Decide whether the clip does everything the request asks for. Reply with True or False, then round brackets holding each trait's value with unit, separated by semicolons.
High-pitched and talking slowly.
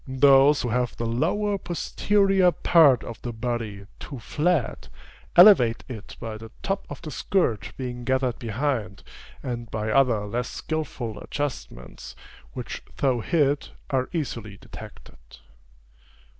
False (125 Hz; 130 wpm)